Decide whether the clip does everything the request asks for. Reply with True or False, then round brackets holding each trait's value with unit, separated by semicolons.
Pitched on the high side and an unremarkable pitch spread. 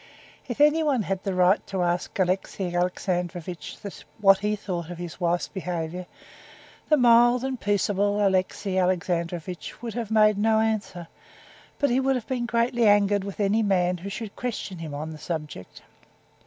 True (195 Hz; 3.8 semitones)